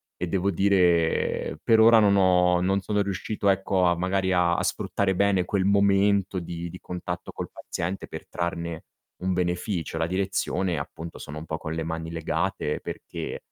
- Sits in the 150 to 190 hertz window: No, very low, 90 Hz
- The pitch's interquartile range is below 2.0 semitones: No, narrow, 2.4 semitones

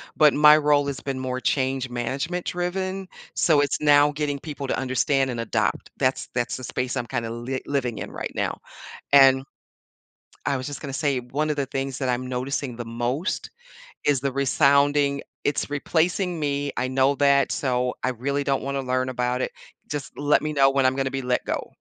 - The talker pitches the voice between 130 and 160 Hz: Yes, low, 135 Hz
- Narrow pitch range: Yes, narrow, 2.0 semitones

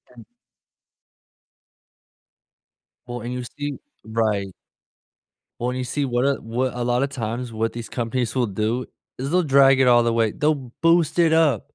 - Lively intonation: No, average, 3.1 semitones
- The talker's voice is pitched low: Yes, low, 125 Hz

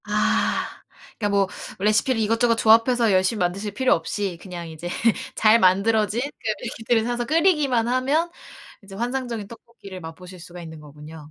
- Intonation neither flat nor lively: Yes, average, 4.6 semitones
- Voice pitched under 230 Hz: Yes, high, 215 Hz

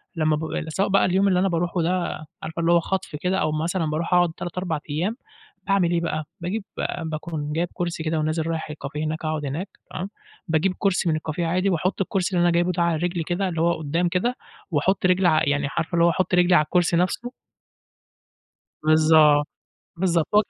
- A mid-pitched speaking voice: Yes, medium, 170 Hz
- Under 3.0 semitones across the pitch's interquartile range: Yes, narrow, 2.6 semitones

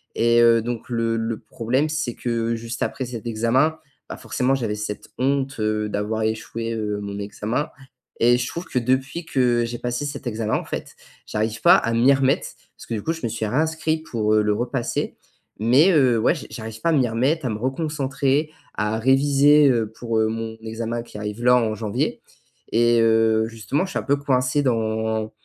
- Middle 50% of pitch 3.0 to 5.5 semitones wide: Yes, average, 3.3 semitones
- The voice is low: Yes, low, 115 Hz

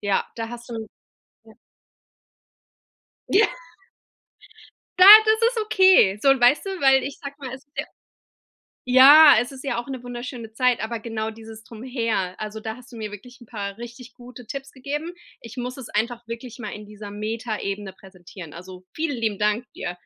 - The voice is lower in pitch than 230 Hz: No, high, 235 Hz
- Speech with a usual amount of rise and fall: Yes, average, 3.4 semitones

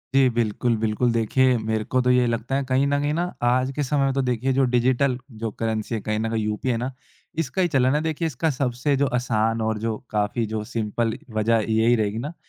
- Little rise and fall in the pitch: No, average, 3.4 semitones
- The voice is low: Yes, low, 120 Hz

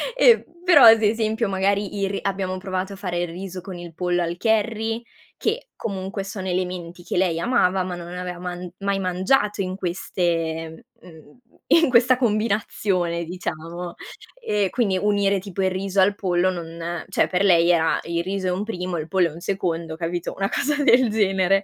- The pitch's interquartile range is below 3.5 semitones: Yes, average, 2.7 semitones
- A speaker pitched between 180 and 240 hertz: Yes, medium, 185 Hz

